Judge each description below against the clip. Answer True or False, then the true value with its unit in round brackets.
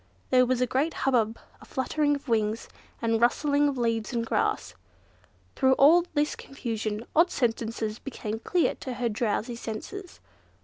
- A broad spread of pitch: False (4.0 semitones)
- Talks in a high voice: True (245 Hz)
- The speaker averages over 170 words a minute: False (150 wpm)